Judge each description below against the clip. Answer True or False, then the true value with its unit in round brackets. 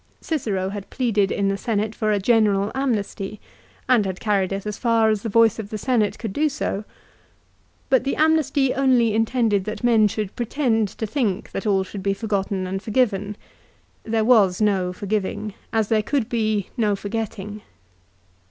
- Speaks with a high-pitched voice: True (215 Hz)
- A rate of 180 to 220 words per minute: False (170 wpm)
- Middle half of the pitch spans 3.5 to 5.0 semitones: False (2.7 semitones)